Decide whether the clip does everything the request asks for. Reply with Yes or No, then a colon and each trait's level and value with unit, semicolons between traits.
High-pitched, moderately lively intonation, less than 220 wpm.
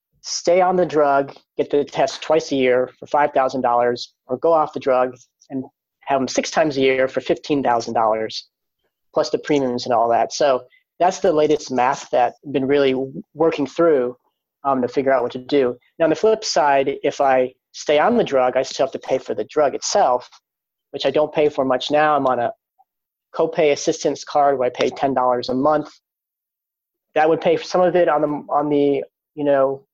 No: medium, 140 Hz; average, 3.0 semitones; fast, 205 wpm